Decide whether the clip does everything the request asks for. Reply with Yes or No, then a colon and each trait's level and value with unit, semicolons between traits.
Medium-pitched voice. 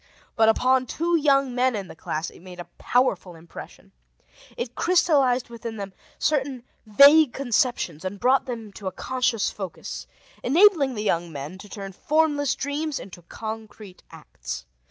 No: high, 240 Hz